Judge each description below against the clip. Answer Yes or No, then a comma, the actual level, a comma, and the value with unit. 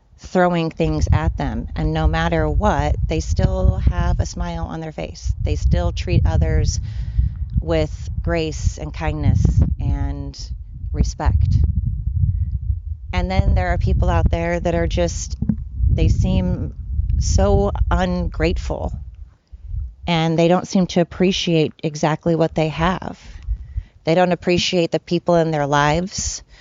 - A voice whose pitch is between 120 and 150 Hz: No, very low, 90 Hz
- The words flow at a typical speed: No, slow, 130 wpm